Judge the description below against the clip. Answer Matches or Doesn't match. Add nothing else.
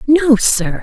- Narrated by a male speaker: Doesn't match